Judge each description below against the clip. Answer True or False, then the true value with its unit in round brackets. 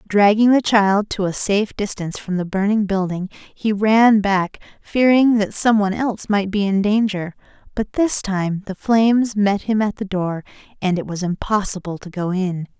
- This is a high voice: True (200 Hz)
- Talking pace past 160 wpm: True (190 wpm)